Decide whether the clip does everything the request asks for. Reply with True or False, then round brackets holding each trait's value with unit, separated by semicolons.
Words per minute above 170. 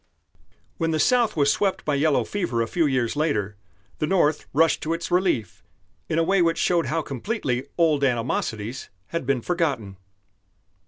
False (165 wpm)